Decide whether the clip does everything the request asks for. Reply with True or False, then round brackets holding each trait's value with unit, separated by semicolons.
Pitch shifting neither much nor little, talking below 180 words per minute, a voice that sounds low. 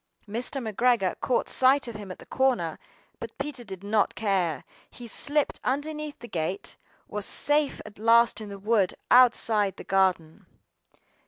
False (4.7 semitones; 160 wpm; 225 Hz)